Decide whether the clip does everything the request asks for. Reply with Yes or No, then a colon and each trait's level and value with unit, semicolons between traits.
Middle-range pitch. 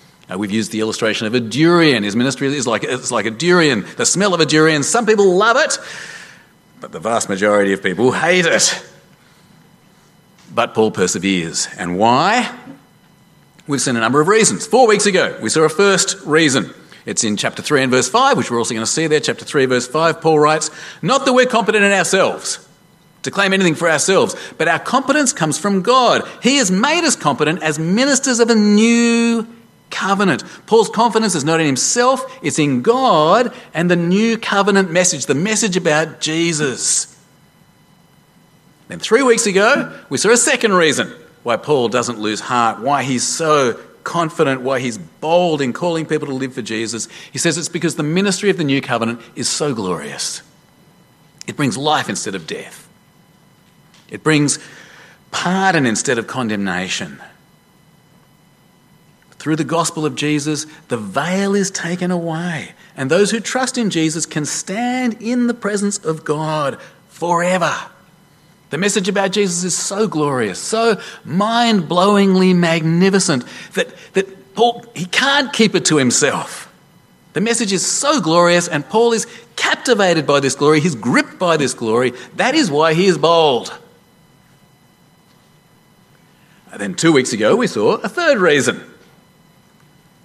Yes: medium, 170 Hz